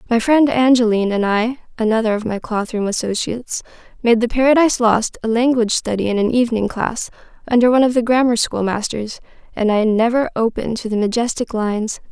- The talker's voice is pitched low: No, high, 230 Hz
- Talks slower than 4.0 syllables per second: No, 5.2 syllables/s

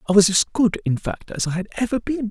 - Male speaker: Yes, male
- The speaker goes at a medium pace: No, fast, 285 wpm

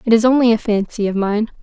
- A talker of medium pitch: No, high, 220 Hz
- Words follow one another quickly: Yes, fast, 260 wpm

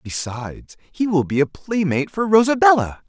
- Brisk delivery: No, average, 155 wpm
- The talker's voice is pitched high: No, medium, 160 Hz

